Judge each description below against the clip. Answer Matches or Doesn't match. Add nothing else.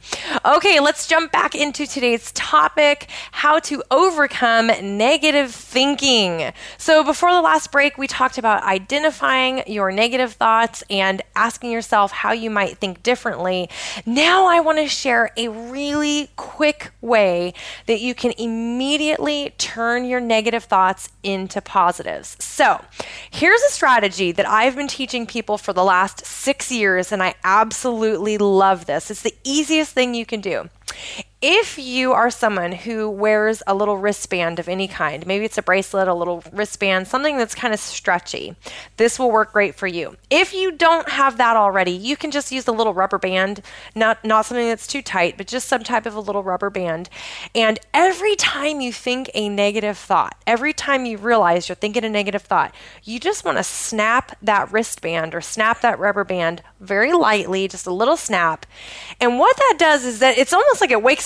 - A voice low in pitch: Doesn't match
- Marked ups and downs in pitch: Doesn't match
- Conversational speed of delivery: Matches